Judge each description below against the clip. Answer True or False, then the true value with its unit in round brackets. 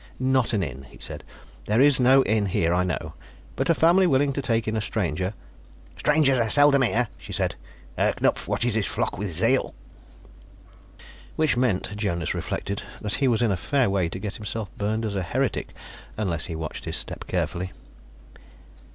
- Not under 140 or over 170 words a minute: False (185 wpm)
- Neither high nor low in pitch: False (110 Hz)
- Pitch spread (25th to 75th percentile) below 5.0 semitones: False (5.5 semitones)